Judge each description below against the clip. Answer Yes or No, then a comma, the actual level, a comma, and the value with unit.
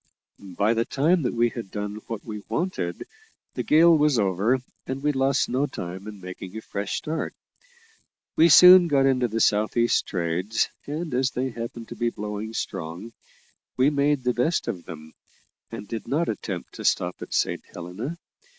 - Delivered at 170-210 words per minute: Yes, average, 180 wpm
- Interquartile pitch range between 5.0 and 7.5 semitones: Yes, wide, 5.4 semitones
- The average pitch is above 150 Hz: No, low, 115 Hz